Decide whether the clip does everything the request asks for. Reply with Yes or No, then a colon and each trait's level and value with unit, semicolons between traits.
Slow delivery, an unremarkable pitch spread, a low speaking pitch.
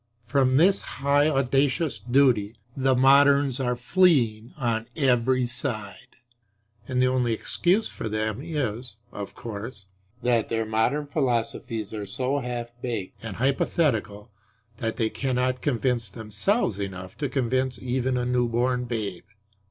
Yes: slow, 130 wpm; average, 3.2 semitones; low, 125 Hz